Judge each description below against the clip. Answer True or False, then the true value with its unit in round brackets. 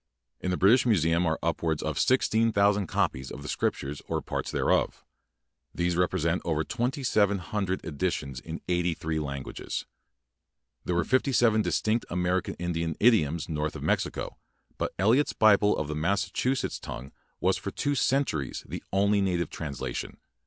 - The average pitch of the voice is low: True (90 Hz)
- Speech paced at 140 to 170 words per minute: True (145 wpm)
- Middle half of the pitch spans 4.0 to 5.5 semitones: True (4.8 semitones)